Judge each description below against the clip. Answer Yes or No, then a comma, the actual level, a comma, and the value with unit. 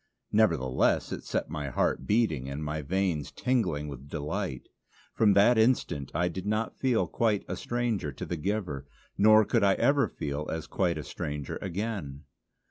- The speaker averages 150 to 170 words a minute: Yes, average, 165 wpm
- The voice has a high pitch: No, very low, 90 Hz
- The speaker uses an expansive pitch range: Yes, wide, 6.7 semitones